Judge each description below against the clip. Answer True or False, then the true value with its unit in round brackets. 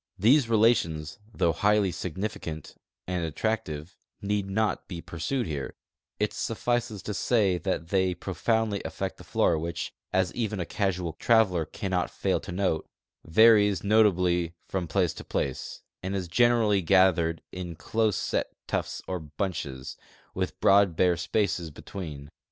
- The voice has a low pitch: True (95 Hz)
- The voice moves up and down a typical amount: True (4.0 semitones)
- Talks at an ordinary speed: True (145 wpm)